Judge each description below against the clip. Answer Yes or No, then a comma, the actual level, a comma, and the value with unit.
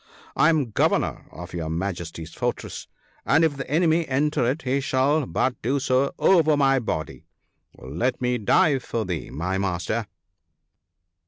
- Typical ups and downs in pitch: No, wide, 7.5 semitones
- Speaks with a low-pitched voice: Yes, low, 130 Hz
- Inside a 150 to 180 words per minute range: Yes, average, 155 wpm